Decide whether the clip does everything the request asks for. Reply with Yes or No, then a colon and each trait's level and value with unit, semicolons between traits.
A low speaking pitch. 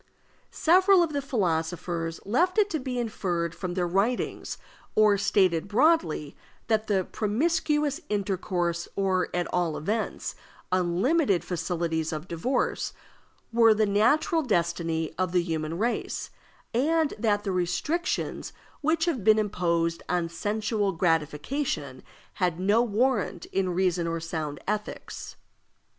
No: high, 195 Hz